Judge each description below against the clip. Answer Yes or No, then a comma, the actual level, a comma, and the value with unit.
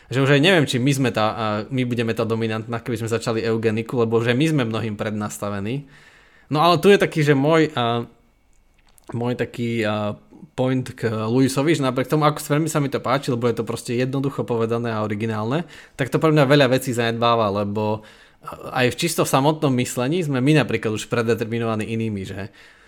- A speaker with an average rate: No, fast, 185 wpm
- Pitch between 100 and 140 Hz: Yes, low, 120 Hz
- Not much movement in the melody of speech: No, average, 3.7 semitones